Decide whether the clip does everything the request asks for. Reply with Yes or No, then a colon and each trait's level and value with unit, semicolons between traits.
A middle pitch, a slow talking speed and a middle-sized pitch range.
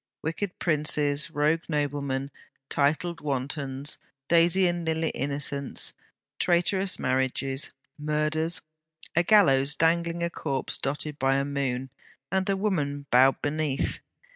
Yes: medium, 150 Hz; slow, 115 wpm; average, 3.3 semitones